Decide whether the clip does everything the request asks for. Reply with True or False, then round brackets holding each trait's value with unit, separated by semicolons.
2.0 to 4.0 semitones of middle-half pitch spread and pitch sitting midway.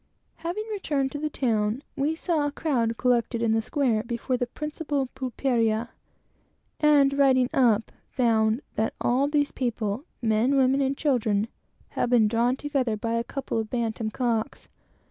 False (3.7 semitones; 250 Hz)